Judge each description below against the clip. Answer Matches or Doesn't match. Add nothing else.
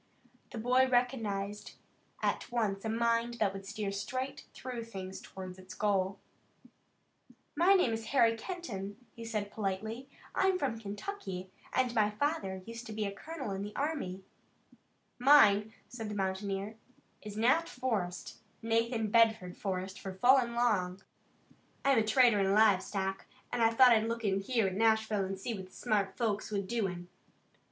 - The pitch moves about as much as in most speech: Matches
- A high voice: Matches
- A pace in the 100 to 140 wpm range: Doesn't match